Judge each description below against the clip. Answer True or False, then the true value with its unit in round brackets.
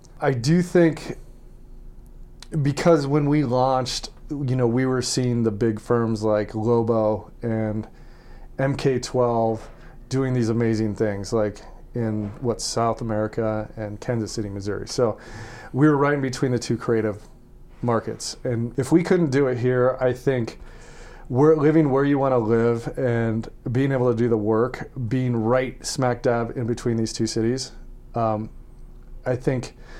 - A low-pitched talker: True (120 Hz)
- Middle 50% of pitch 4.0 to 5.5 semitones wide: False (2.9 semitones)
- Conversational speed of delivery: True (155 wpm)